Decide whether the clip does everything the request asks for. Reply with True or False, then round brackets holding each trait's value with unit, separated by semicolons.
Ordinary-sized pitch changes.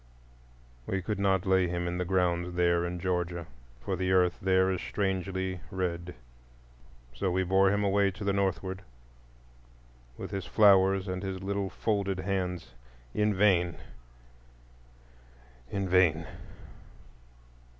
False (1.6 semitones)